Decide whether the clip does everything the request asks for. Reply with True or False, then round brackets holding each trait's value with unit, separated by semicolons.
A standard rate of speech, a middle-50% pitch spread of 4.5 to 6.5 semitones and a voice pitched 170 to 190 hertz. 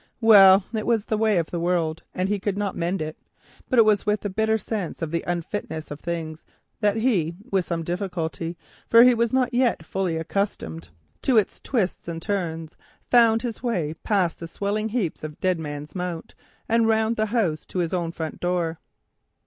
True (190 wpm; 4.9 semitones; 185 Hz)